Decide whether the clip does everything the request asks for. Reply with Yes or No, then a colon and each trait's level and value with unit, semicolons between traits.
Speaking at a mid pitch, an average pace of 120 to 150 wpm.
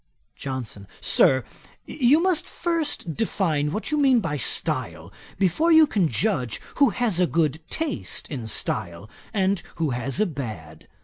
Yes: medium, 165 Hz; average, 145 wpm